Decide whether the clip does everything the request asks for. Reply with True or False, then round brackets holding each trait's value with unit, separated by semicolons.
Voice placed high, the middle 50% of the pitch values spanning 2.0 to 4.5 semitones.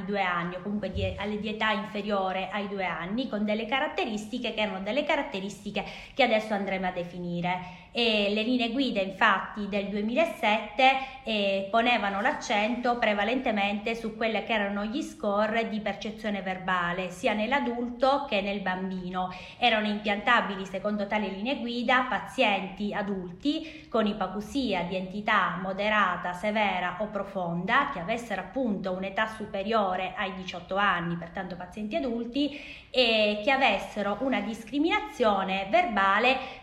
True (210 Hz; 3.3 semitones)